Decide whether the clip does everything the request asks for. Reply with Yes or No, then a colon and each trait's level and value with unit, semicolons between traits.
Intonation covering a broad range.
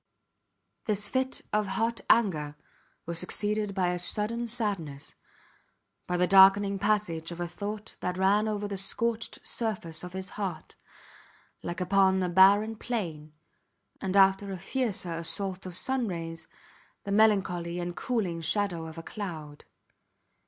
No: average, 3.3 semitones